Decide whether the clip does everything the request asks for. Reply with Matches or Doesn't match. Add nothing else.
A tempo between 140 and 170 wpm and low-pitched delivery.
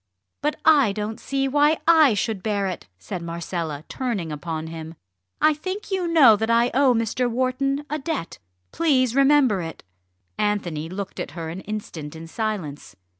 Doesn't match